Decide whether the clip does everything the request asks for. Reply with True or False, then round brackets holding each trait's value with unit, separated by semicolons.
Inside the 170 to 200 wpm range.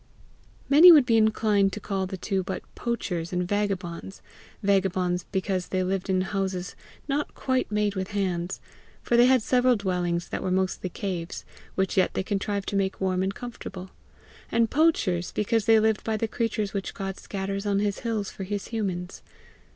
True (175 wpm)